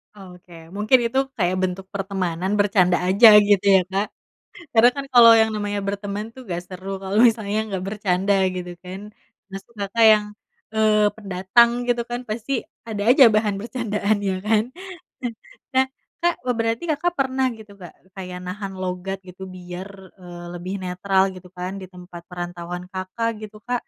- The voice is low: No, high, 200 Hz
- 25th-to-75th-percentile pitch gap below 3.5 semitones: Yes, average, 3.1 semitones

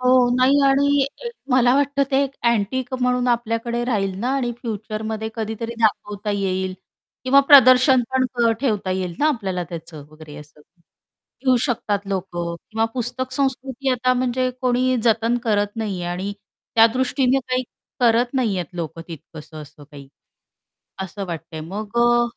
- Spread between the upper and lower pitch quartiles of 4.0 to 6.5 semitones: Yes, average, 4.9 semitones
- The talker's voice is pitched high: Yes, high, 230 Hz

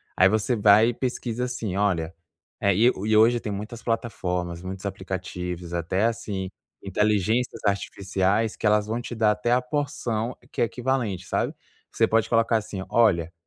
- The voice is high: No, low, 105 Hz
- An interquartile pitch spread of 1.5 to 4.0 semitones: Yes, average, 3.6 semitones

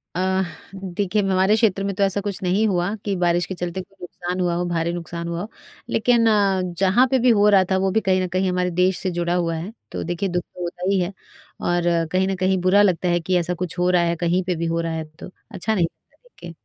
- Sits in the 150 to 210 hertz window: Yes, medium, 185 Hz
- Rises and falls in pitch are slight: Yes, narrow, 1.9 semitones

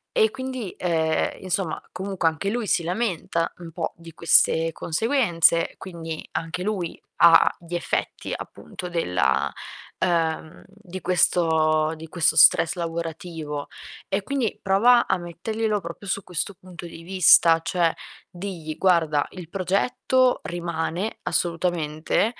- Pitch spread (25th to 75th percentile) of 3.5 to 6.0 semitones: No, average, 2.9 semitones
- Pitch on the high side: No, medium, 175 Hz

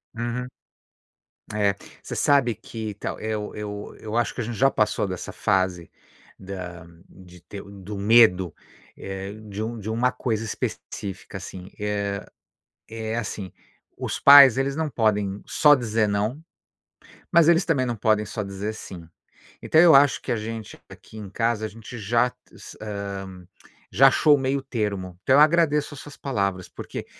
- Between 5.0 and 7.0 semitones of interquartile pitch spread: No, average, 4.0 semitones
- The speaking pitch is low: Yes, low, 110 Hz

